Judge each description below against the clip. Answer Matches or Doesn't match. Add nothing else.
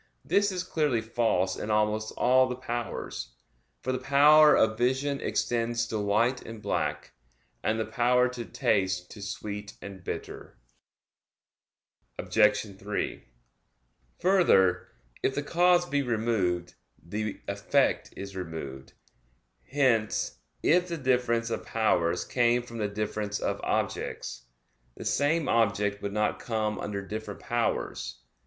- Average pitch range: Matches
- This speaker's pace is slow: Matches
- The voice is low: Matches